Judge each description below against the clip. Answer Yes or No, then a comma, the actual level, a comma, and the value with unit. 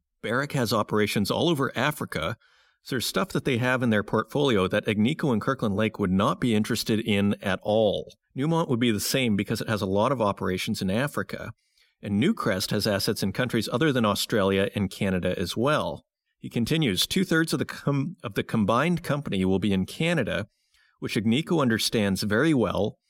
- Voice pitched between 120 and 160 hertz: No, low, 110 Hz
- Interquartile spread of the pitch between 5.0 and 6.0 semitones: Yes, average, 5.3 semitones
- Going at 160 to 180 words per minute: No, average, 190 wpm